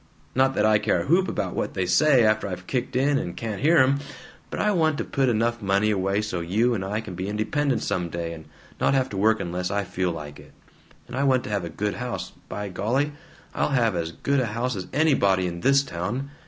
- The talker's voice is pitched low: Yes, low, 110 Hz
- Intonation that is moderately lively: No, wide, 6.0 semitones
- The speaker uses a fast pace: Yes, fast, 235 wpm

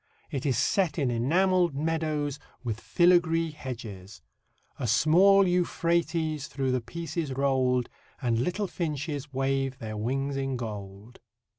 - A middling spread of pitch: Yes, average, 4.8 semitones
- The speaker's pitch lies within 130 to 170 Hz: Yes, medium, 140 Hz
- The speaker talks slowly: Yes, slow, 130 wpm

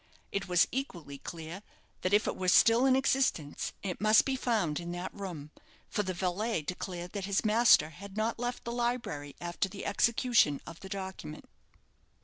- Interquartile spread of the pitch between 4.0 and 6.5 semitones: Yes, average, 4.8 semitones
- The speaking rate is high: No, average, 175 wpm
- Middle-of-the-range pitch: No, high, 195 Hz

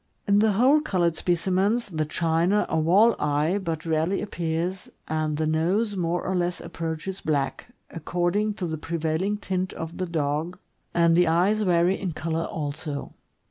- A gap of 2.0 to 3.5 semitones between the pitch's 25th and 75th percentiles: Yes, average, 3.1 semitones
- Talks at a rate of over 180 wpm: No, average, 160 wpm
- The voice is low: No, medium, 170 Hz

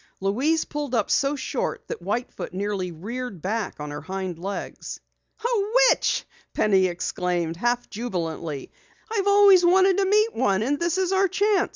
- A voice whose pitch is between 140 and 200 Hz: No, high, 235 Hz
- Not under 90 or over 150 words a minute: No, average, 165 wpm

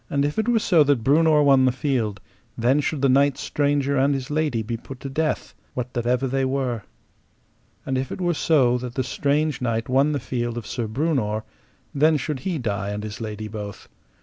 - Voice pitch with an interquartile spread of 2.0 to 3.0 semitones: No, average, 3.4 semitones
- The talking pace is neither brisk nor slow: No, fast, 210 wpm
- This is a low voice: Yes, low, 130 Hz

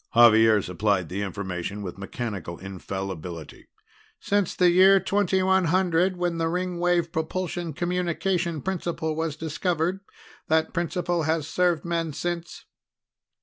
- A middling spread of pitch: No, wide, 8.4 semitones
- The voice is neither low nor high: Yes, medium, 165 Hz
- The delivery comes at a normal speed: No, slow, 110 wpm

